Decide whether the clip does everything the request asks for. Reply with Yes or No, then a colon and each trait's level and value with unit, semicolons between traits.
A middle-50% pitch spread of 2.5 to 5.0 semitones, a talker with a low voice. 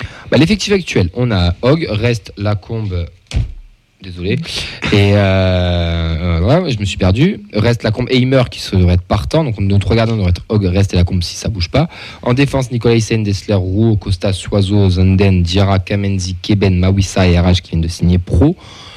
Yes: average, 3.6 semitones; low, 100 Hz